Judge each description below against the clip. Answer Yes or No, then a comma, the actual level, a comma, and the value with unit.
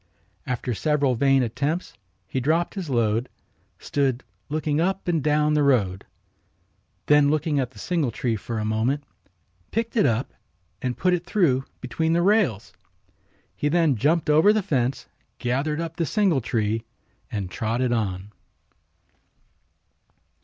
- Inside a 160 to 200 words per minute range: No, slow, 135 wpm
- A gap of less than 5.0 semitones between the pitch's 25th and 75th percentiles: No, average, 5.3 semitones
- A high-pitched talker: No, medium, 140 Hz